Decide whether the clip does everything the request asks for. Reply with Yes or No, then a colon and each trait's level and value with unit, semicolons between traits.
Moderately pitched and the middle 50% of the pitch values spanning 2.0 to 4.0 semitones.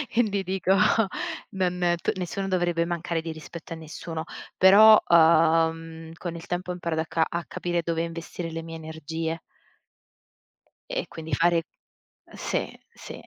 No: medium, 170 Hz; narrow, 1.6 semitones